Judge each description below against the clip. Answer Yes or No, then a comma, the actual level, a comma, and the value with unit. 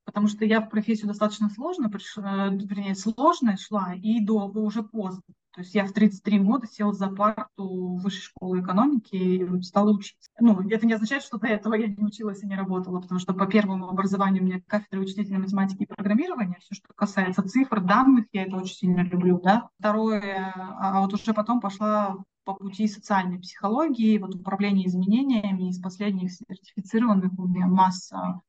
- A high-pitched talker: Yes, high, 200 Hz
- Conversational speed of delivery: No, fast, 180 wpm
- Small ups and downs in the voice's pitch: Yes, narrow, 2.1 semitones